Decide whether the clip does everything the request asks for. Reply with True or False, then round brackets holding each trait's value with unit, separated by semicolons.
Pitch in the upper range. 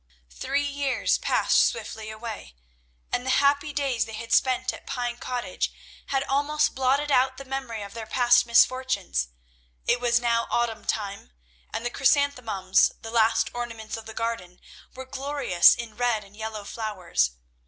True (240 Hz)